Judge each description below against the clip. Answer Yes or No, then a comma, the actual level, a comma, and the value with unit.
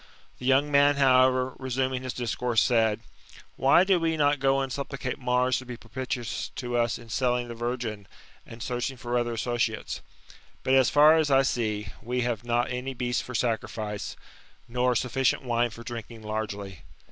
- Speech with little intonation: Yes, narrow, 2.0 semitones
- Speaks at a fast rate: No, average, 170 wpm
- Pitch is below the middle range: Yes, low, 125 Hz